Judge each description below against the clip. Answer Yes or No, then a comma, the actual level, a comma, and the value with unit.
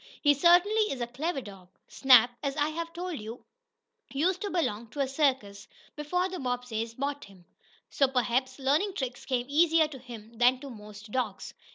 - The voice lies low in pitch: No, very high, 265 Hz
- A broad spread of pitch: No, average, 4.7 semitones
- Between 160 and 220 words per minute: Yes, average, 180 wpm